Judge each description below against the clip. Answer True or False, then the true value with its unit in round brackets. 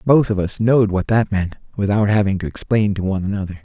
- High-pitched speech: False (100 Hz)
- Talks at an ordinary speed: False (230 wpm)